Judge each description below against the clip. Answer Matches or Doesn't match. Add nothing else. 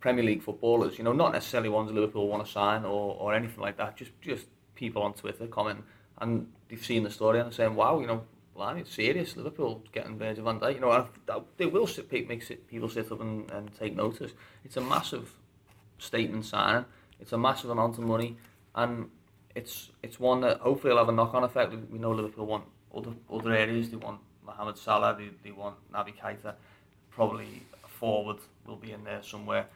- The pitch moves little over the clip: Matches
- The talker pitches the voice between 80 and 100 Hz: Doesn't match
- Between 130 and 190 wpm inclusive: Doesn't match